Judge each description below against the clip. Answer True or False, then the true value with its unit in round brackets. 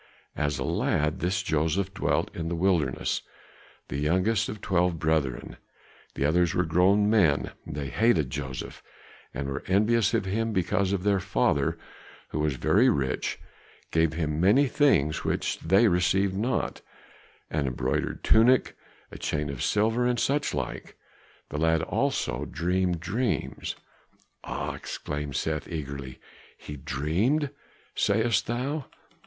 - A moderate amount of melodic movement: False (5.8 semitones)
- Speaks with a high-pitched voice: False (90 Hz)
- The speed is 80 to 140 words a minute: True (135 wpm)